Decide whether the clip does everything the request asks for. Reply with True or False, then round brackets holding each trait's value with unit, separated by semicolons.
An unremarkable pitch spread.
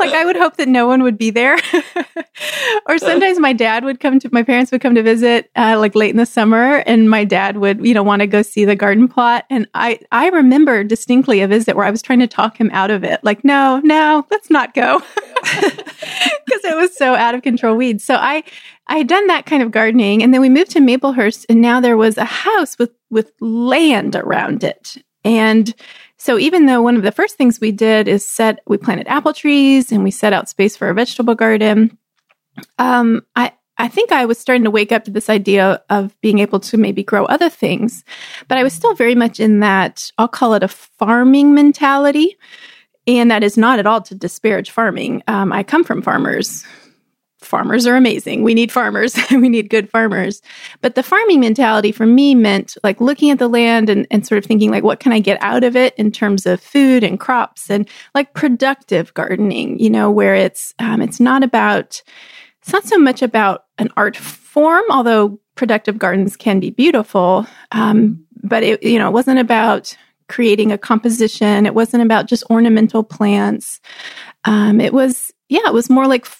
True (3.8 semitones)